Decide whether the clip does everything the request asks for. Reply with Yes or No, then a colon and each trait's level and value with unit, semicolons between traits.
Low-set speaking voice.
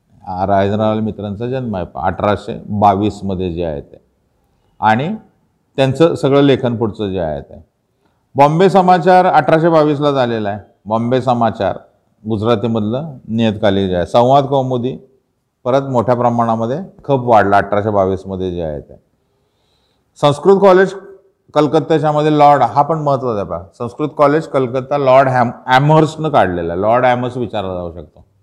Yes: low, 125 Hz